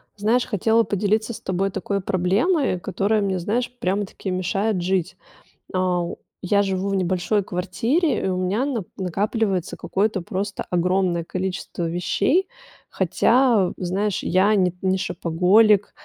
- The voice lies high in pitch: Yes, high, 195 Hz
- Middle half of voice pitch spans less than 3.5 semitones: Yes, average, 2.7 semitones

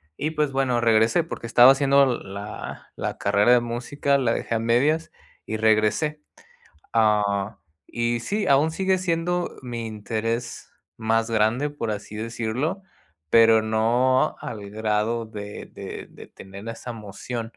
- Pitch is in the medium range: No, low, 115 Hz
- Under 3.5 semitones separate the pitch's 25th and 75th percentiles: No, average, 3.9 semitones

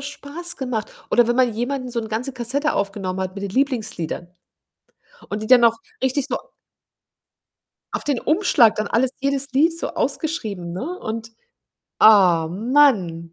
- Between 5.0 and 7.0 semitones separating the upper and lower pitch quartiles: Yes, wide, 5.4 semitones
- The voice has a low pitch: No, high, 240 Hz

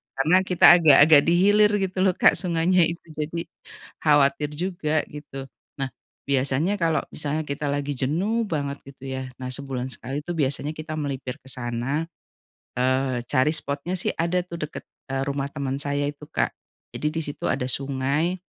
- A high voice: No, medium, 145 Hz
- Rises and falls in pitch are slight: No, average, 3.5 semitones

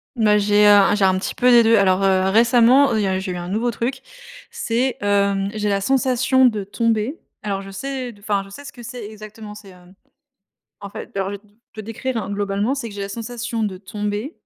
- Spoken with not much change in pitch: No, average, 3.2 semitones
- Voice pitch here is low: No, high, 210 Hz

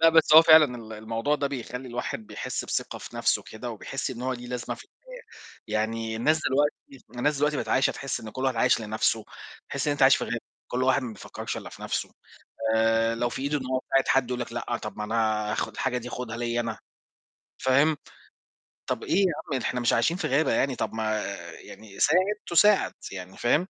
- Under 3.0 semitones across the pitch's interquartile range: No, average, 3.7 semitones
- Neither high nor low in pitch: No, low, 125 Hz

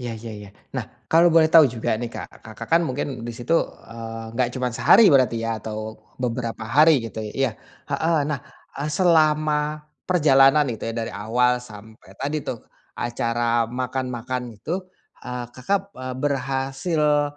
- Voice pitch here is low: Yes, low, 125 Hz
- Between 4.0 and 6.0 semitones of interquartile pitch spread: Yes, average, 4.4 semitones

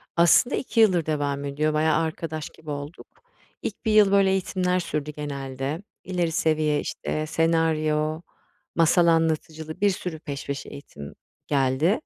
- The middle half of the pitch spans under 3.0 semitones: Yes, narrow, 2.6 semitones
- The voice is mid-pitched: Yes, medium, 155 Hz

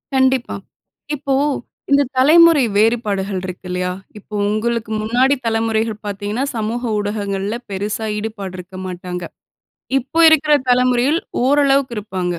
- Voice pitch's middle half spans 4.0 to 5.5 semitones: Yes, average, 4.5 semitones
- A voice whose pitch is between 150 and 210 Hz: No, high, 220 Hz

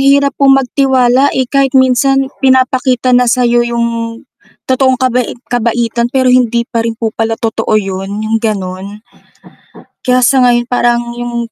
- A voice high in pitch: Yes, high, 240 Hz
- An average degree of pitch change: No, narrow, 2.2 semitones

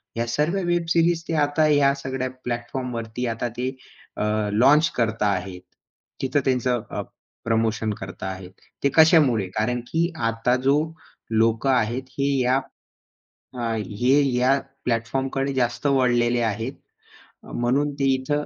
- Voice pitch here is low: Yes, low, 125 Hz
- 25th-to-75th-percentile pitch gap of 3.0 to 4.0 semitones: Yes, average, 3.4 semitones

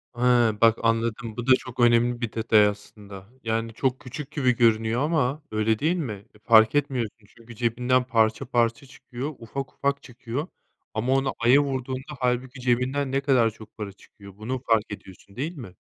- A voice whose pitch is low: Yes, low, 120 Hz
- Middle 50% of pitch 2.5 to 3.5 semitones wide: Yes, average, 2.9 semitones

